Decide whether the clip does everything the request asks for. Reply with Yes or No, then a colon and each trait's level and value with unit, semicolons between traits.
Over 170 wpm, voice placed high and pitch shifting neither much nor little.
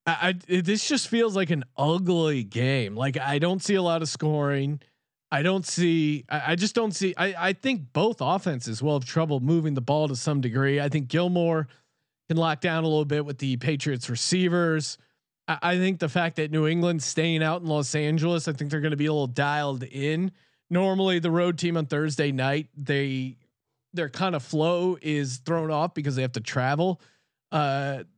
No: fast, 205 wpm; medium, 155 Hz; average, 3.5 semitones